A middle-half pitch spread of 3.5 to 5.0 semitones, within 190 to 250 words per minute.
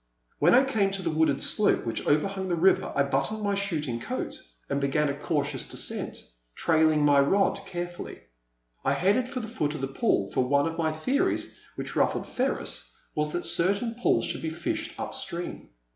No: wide, 5.4 semitones; average, 200 wpm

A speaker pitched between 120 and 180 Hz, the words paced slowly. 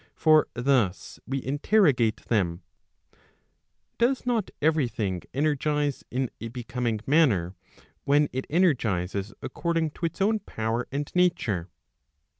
Yes: low, 135 Hz; slow, 115 wpm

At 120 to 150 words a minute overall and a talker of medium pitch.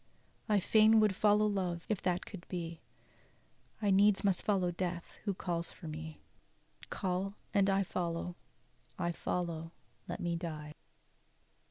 Yes: average, 140 wpm; medium, 180 Hz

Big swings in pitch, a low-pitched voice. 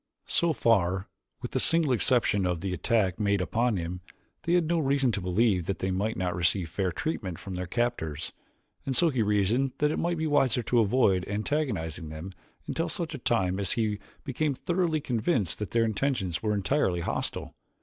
Yes: wide, 6.7 semitones; low, 110 Hz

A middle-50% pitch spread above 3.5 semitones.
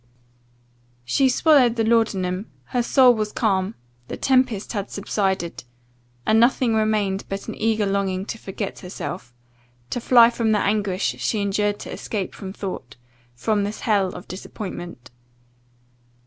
No: average, 2.8 semitones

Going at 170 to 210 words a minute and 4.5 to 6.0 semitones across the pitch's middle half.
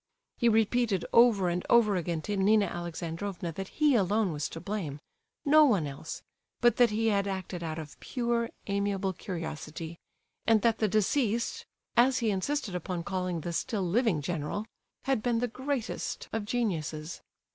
No: average, 155 wpm; average, 5.1 semitones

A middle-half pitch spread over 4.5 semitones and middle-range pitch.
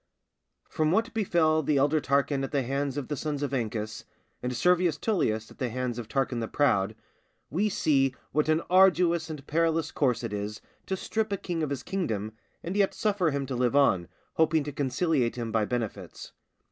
Yes: average, 5.1 semitones; medium, 145 Hz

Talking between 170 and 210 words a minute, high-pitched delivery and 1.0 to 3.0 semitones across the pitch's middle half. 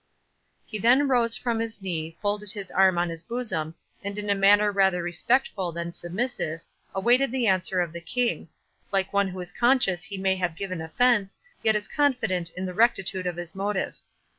No: average, 185 wpm; high, 195 Hz; average, 4.2 semitones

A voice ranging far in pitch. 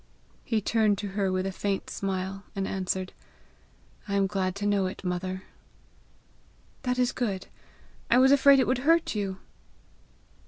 No: average, 4.2 semitones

